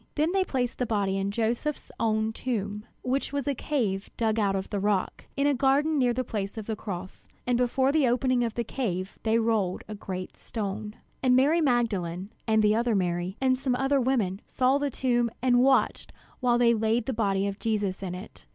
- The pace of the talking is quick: Yes, fast, 210 wpm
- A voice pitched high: Yes, high, 230 Hz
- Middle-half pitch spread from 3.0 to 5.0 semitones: Yes, average, 4.2 semitones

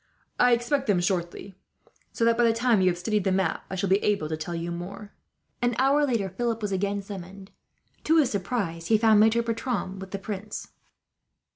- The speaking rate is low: No, fast, 205 wpm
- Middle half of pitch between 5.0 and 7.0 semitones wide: No, average, 3.7 semitones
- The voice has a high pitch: Yes, high, 200 Hz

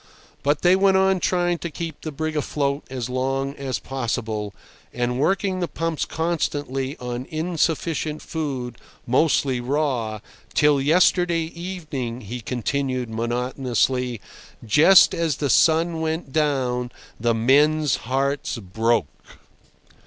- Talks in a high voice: No, medium, 140 Hz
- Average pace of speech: No, slow, 120 wpm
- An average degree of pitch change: Yes, average, 4.5 semitones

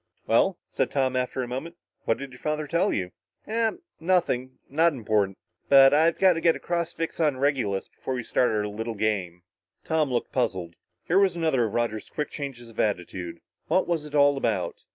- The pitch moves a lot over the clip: Yes, wide, 6.7 semitones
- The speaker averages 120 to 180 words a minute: No, average, 195 wpm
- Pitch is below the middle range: Yes, low, 130 Hz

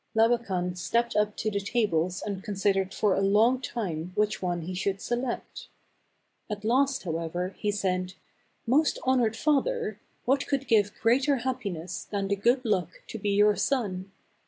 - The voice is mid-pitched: No, high, 210 Hz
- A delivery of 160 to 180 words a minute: Yes, average, 170 wpm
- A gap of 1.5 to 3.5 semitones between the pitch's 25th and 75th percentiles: No, average, 4.2 semitones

